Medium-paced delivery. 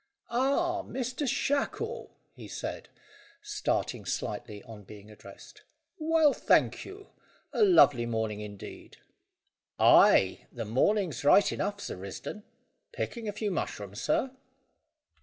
No: slow, 115 wpm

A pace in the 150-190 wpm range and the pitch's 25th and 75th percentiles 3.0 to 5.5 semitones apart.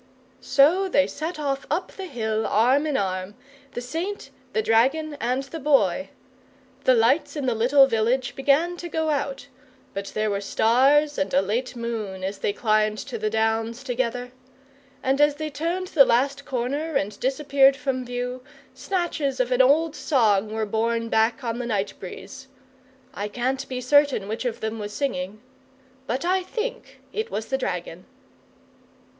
Yes: average, 165 wpm; average, 4.6 semitones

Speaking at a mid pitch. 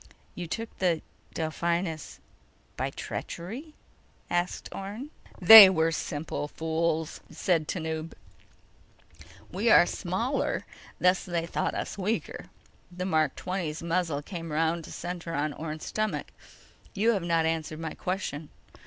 Yes: medium, 170 Hz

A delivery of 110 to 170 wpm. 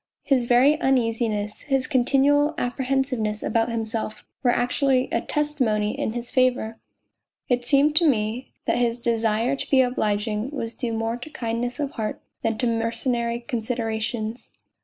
Yes: average, 160 wpm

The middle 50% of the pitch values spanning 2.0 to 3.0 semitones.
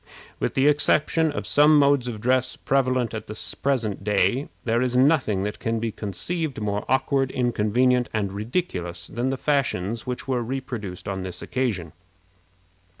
No: average, 4.3 semitones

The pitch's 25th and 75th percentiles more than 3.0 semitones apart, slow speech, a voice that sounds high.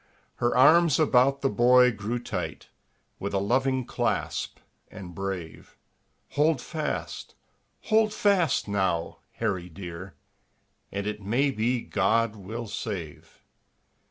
No: average, 5.3 semitones; slow, 115 wpm; low, 115 Hz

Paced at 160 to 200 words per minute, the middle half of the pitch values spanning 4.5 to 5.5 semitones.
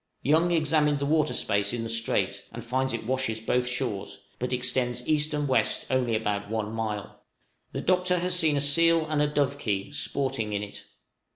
Yes: average, 185 wpm; average, 5.0 semitones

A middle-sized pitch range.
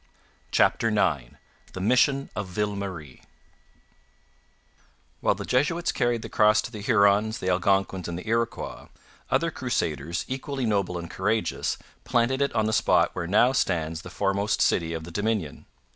Yes: average, 4.5 semitones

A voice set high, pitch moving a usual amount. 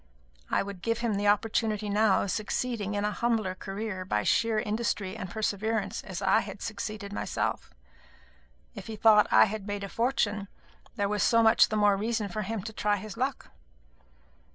No: high, 210 Hz; narrow, 1.8 semitones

